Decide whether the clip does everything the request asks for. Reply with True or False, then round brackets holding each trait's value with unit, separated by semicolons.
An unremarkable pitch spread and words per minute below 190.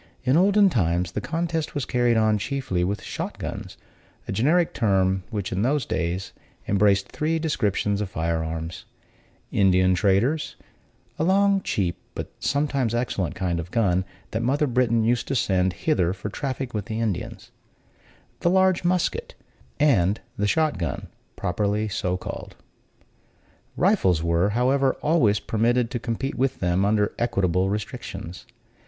False (6.4 semitones; 145 wpm)